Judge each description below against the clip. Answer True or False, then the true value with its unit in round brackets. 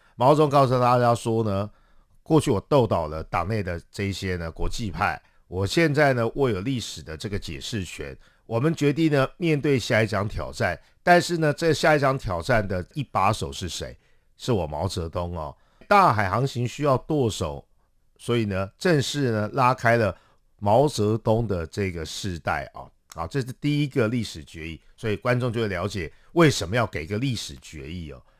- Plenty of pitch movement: True (6.7 semitones)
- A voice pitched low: True (110 Hz)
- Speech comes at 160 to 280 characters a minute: True (265 characters per minute)